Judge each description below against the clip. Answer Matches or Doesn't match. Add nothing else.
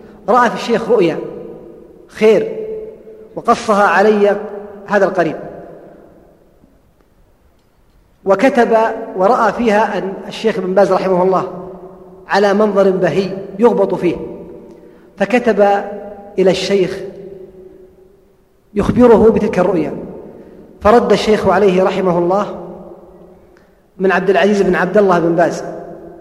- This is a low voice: Doesn't match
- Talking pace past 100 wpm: Doesn't match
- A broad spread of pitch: Doesn't match